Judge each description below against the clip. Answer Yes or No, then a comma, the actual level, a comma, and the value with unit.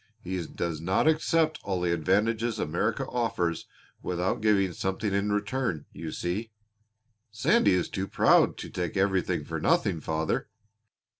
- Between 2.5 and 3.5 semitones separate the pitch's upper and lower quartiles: No, average, 4.1 semitones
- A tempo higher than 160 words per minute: No, average, 140 wpm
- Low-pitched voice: Yes, very low, 95 Hz